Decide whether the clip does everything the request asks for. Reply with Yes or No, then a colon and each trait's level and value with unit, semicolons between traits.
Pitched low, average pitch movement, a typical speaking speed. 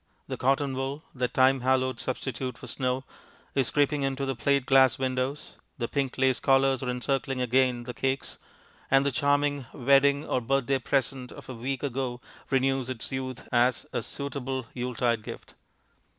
No: low, 130 Hz; narrow, 1.3 semitones; average, 165 wpm